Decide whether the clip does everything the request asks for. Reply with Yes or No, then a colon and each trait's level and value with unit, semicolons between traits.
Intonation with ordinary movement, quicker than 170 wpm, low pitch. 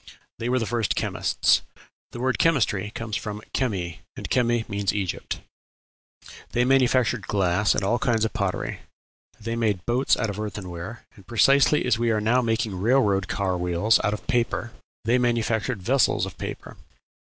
No: average, 3.1 semitones; average, 160 wpm; low, 110 Hz